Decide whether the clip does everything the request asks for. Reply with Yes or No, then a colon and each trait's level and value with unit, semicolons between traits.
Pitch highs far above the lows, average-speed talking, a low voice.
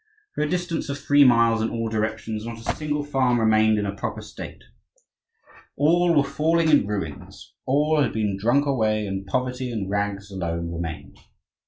Yes: wide, 5.9 semitones; average, 175 wpm; low, 115 Hz